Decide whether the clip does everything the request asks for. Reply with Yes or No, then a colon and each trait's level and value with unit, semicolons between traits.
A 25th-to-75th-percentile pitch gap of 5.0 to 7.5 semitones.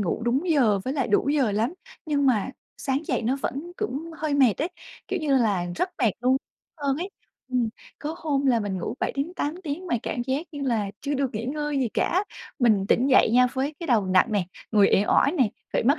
No: average, 4.4 semitones